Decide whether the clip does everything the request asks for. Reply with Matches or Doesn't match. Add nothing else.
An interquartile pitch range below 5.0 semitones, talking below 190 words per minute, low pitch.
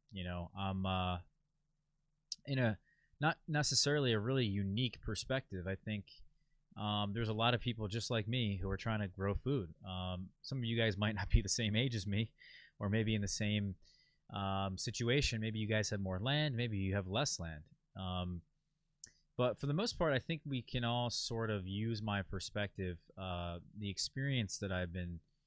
Doesn't match